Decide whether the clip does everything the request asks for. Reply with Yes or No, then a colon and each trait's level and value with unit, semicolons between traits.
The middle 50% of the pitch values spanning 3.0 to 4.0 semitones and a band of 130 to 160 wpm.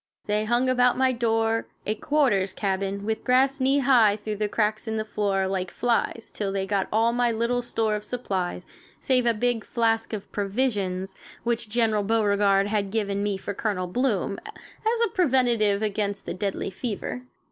No: average, 3.3 semitones; average, 175 wpm